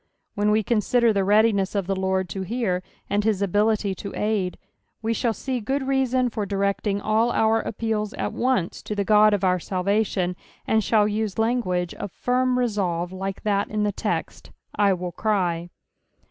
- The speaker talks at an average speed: Yes, average, 180 wpm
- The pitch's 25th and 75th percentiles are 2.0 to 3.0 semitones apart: Yes, average, 2.7 semitones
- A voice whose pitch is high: Yes, high, 210 Hz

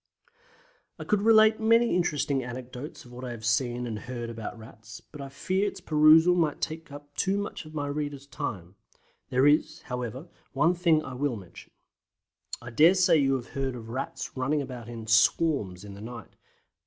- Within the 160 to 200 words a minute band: Yes, average, 185 wpm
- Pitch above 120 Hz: Yes, low, 135 Hz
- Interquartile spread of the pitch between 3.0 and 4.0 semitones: No, average, 4.9 semitones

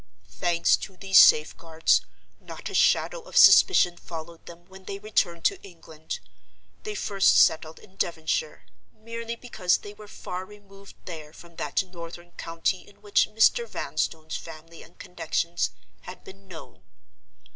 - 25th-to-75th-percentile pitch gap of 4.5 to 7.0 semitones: No, average, 3.3 semitones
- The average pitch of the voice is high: No, medium, 180 Hz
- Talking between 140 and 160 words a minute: Yes, average, 145 wpm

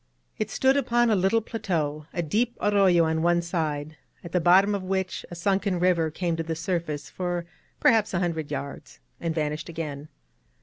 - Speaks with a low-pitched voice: No, medium, 175 Hz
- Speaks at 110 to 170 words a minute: No, average, 180 wpm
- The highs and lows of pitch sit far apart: No, average, 3.4 semitones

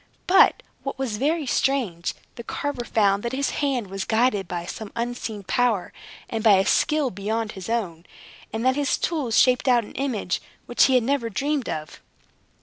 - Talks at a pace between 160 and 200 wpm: Yes, average, 180 wpm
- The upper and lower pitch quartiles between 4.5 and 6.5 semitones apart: Yes, average, 4.8 semitones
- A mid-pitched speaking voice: No, high, 235 Hz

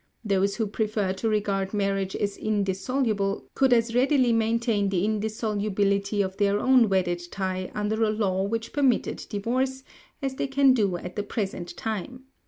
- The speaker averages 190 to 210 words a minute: No, average, 160 wpm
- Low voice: No, high, 210 Hz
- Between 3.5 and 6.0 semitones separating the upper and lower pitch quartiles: No, average, 2.8 semitones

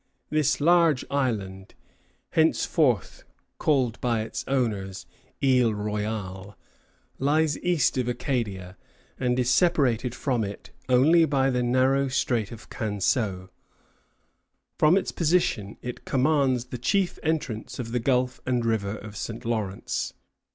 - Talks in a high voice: No, low, 125 Hz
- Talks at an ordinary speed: No, slow, 125 wpm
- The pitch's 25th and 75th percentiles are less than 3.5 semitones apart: No, average, 4.2 semitones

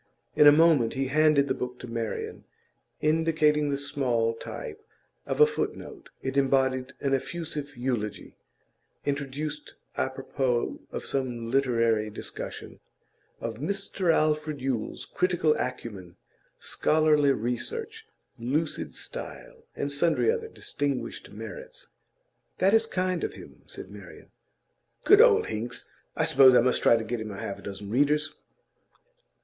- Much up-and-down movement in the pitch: No, average, 5.0 semitones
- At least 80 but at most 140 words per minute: Yes, slow, 135 wpm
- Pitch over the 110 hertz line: Yes, medium, 140 Hz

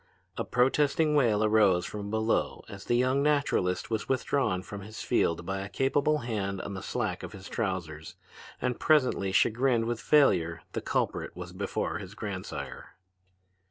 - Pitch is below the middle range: Yes, low, 110 Hz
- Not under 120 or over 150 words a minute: No, average, 160 wpm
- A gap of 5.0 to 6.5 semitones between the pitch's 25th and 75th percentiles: Yes, average, 5.3 semitones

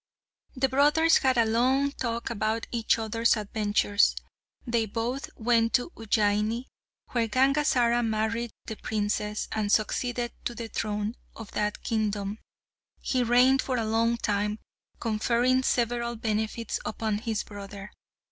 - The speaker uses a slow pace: Yes, slow, 130 wpm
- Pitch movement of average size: No, narrow, 2.3 semitones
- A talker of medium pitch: No, high, 230 Hz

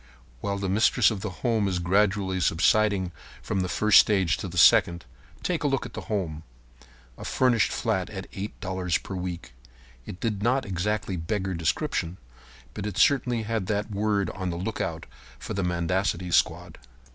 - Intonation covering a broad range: No, average, 3.0 semitones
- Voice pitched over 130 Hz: No, very low, 95 Hz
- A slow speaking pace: No, average, 170 wpm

